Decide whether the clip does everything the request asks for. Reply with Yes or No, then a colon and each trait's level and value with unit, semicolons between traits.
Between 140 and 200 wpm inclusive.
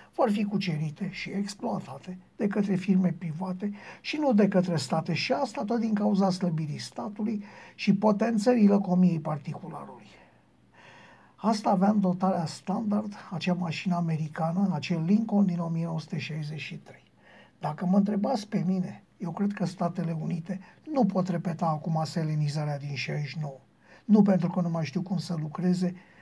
Yes: average, 145 wpm